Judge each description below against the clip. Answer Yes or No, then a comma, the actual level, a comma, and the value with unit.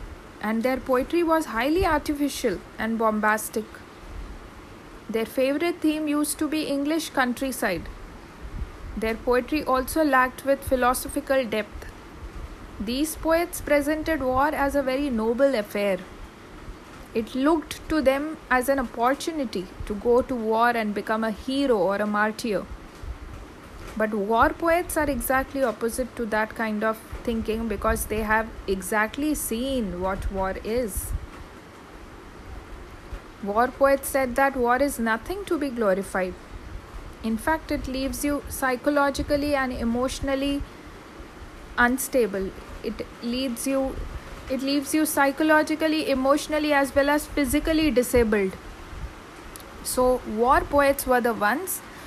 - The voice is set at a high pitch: Yes, very high, 255 Hz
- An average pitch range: Yes, average, 4.6 semitones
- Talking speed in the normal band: No, slow, 125 wpm